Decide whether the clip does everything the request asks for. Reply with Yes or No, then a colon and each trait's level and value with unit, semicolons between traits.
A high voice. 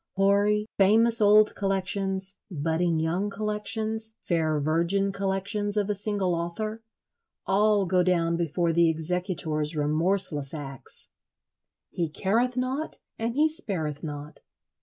Yes: high, 195 Hz